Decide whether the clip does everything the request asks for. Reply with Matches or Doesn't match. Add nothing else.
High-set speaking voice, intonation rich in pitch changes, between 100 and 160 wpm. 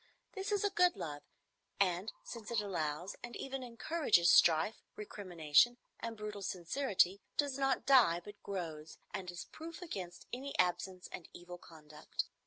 Matches